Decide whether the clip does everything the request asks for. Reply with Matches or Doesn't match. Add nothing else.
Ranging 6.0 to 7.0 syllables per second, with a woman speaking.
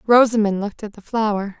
Matches